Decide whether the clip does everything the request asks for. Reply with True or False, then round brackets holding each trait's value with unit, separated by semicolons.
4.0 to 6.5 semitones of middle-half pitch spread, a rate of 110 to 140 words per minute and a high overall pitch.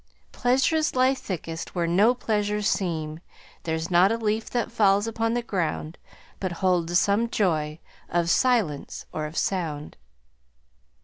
True (5.3 semitones; 135 wpm; 195 Hz)